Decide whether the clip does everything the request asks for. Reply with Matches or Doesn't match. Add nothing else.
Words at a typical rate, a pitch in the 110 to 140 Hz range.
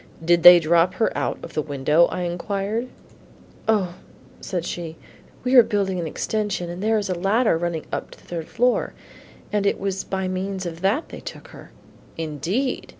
Doesn't match